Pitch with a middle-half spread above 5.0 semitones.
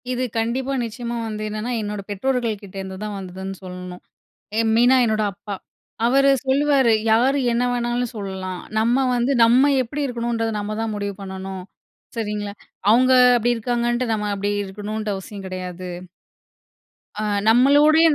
No: average, 3.5 semitones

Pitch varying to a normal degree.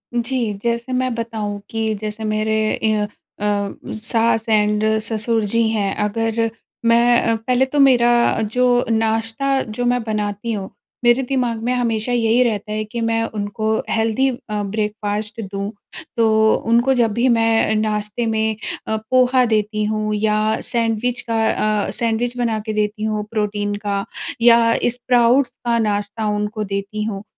No: narrow, 1.9 semitones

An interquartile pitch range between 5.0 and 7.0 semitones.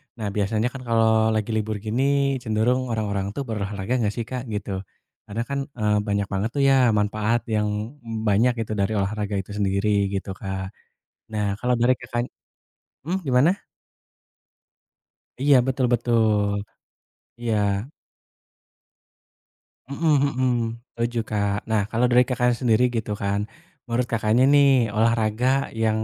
No: average, 3.2 semitones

